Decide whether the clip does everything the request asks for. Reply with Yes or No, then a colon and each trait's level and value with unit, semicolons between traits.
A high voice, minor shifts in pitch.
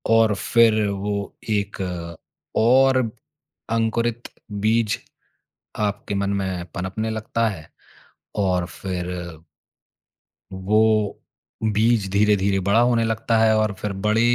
No: low, 105 Hz; narrow, 2.3 semitones